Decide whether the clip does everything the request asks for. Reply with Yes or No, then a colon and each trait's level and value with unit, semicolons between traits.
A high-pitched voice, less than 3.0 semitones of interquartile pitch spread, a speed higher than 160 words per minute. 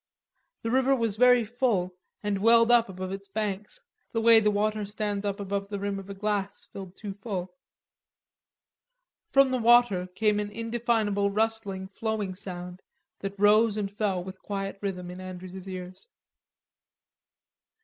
No: high, 205 Hz; narrow, 2.6 semitones; average, 150 wpm